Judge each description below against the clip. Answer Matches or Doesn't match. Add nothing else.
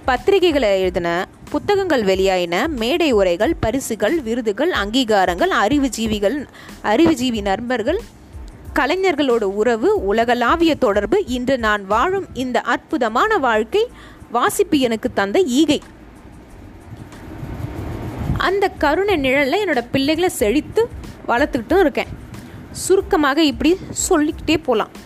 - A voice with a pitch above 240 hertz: Matches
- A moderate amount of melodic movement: Doesn't match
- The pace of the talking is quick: Doesn't match